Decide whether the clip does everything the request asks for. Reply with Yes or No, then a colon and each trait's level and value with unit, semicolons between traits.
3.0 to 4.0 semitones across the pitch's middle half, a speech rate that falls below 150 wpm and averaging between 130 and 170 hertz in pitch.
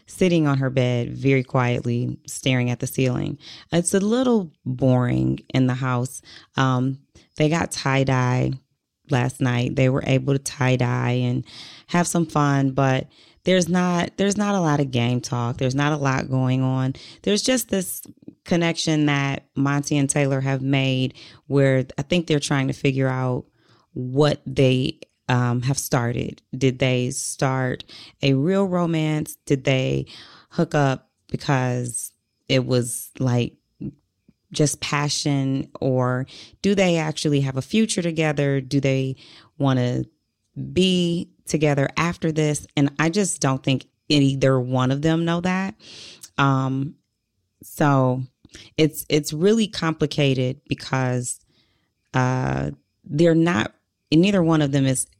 Yes: average, 3.4 semitones; average, 140 wpm; low, 135 Hz